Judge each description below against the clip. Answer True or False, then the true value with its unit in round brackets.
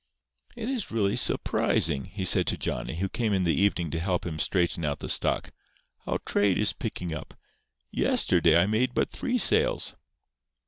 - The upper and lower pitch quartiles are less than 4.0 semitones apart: False (5.1 semitones)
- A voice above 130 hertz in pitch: False (95 Hz)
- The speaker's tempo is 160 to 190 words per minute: True (180 wpm)